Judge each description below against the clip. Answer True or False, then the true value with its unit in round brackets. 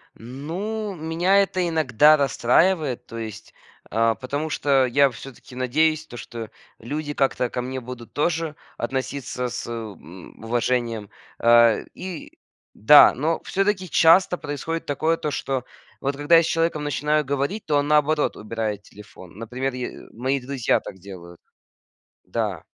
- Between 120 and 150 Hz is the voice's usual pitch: True (140 Hz)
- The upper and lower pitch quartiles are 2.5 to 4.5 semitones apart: False (4.9 semitones)